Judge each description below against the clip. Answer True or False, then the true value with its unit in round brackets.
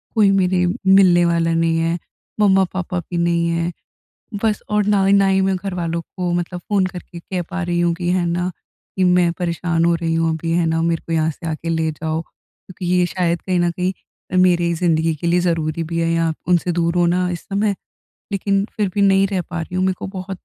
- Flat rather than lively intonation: True (2.0 semitones)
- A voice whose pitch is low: False (175 Hz)